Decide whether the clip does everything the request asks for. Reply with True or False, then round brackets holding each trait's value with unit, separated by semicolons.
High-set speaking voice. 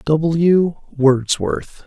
False (150 Hz)